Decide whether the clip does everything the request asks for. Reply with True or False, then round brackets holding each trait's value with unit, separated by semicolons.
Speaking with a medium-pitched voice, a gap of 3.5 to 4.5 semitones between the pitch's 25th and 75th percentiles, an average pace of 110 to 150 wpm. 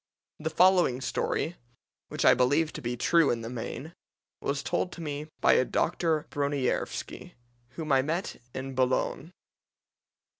True (145 Hz; 4.1 semitones; 140 wpm)